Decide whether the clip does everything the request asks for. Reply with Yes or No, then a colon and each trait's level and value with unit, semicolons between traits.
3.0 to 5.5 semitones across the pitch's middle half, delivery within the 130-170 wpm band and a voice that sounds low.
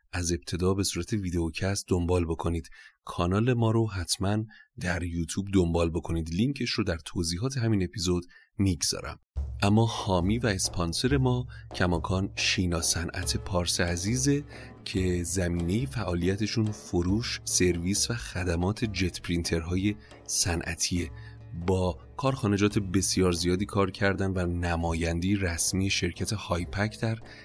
No: average, 3.9 semitones; average, 120 wpm; very low, 95 Hz